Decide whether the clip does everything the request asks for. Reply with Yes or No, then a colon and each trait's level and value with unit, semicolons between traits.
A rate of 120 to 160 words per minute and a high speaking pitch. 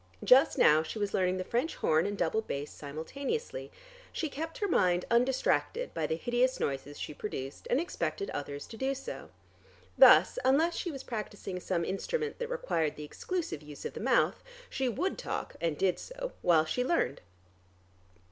No: average, 175 wpm; high, 225 Hz